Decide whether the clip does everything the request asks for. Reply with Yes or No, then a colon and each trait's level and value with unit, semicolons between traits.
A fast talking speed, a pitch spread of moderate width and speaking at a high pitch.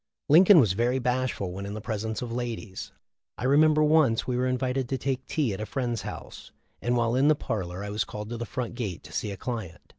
No: fast, 235 wpm; average, 3.7 semitones; low, 120 Hz